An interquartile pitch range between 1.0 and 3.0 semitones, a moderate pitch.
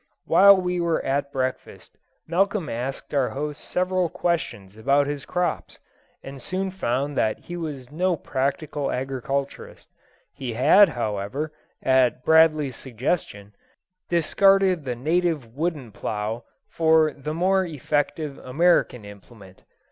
No: average, 5.2 semitones; medium, 145 Hz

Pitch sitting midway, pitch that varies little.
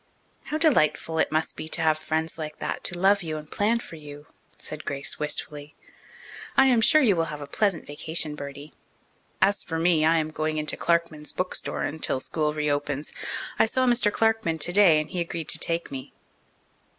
No: medium, 160 Hz; average, 3.3 semitones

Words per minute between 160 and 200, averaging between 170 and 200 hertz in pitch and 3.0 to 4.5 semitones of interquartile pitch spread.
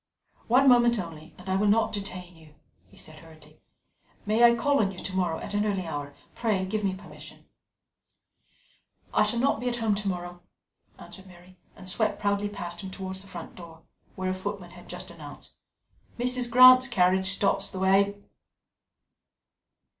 Yes: average, 175 wpm; high, 190 Hz; average, 3.3 semitones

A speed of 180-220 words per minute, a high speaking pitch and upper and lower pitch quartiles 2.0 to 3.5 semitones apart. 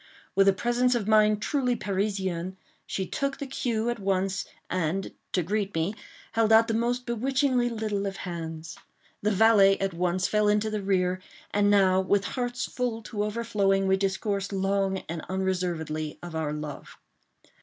No: average, 165 wpm; high, 200 Hz; average, 3.1 semitones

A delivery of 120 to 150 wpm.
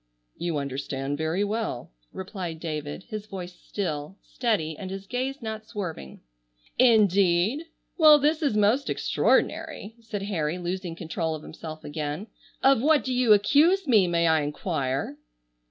Yes: average, 140 wpm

